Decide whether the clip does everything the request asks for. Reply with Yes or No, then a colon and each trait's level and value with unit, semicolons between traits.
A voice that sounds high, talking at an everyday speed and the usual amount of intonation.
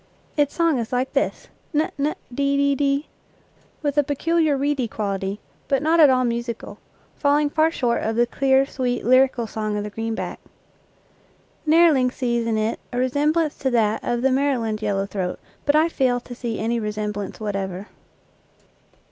Yes: very high, 255 Hz; average, 175 wpm; average, 4.4 semitones